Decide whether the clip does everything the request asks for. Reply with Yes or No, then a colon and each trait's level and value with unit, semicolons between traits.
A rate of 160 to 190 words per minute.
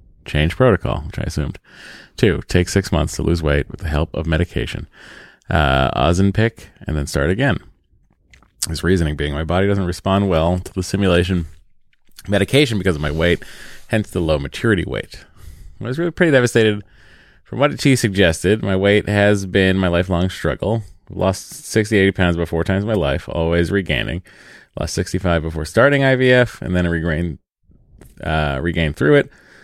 Yes: average, 175 wpm